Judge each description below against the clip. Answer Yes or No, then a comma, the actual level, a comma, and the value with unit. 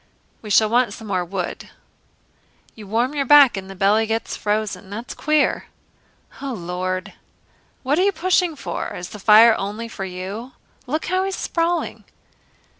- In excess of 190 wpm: No, average, 160 wpm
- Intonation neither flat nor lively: No, wide, 6.5 semitones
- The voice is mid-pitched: No, high, 225 Hz